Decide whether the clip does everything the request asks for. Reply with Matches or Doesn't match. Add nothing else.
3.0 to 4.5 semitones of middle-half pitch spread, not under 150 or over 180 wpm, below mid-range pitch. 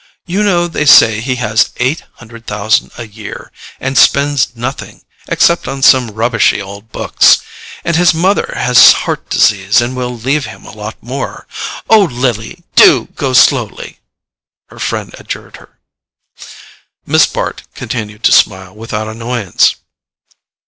Doesn't match